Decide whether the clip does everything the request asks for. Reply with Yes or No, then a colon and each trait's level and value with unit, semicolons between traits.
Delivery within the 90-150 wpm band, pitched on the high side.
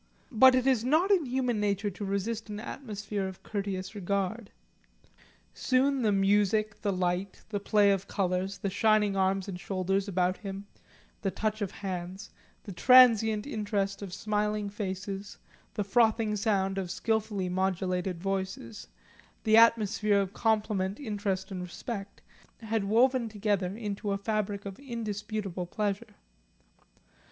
Yes: average, 140 wpm; high, 205 Hz